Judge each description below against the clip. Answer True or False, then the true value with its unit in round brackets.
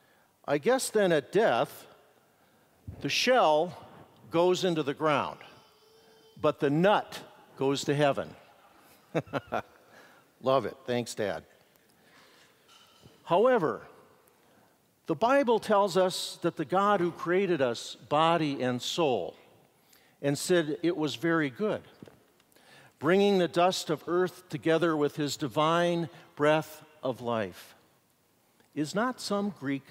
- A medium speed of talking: False (115 wpm)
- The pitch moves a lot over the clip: False (4.7 semitones)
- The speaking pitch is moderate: True (165 Hz)